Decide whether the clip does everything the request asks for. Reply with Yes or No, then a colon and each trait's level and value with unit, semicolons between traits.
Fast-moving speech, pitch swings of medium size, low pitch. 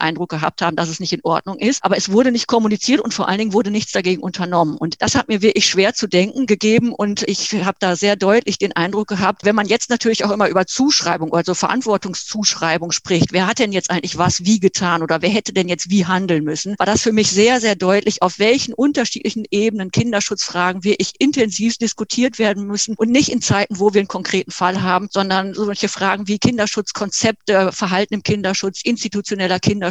No: fast, 215 wpm; average, 3.0 semitones; high, 200 Hz